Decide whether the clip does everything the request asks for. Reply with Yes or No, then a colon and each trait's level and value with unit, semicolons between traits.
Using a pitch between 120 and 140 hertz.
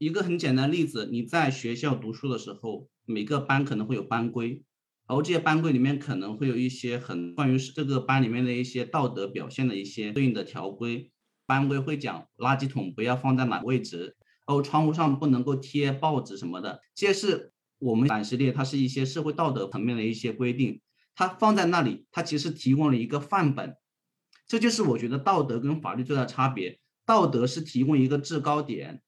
Yes: low, 135 Hz